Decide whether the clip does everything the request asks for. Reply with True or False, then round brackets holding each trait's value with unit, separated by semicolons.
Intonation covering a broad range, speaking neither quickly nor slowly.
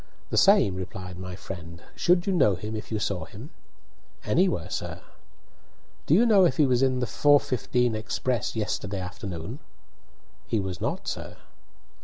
True (6.2 semitones; 155 wpm)